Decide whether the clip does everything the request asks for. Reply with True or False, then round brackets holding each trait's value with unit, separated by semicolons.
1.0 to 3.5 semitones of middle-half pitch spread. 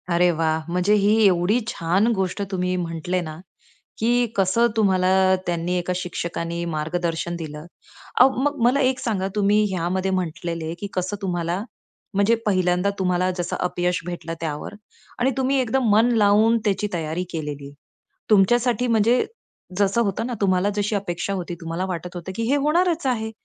False (3.9 semitones)